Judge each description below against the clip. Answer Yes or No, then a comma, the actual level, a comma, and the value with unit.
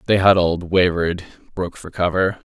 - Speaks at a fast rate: No, average, 145 wpm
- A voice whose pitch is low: Yes, very low, 90 Hz